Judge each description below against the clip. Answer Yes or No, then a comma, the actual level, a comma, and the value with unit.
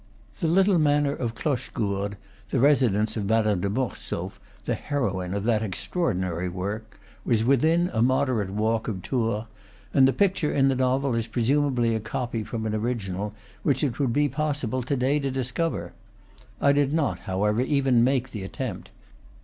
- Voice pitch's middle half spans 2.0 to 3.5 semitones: No, average, 4.5 semitones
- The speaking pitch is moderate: No, low, 120 Hz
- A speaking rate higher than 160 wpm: Yes, average, 170 wpm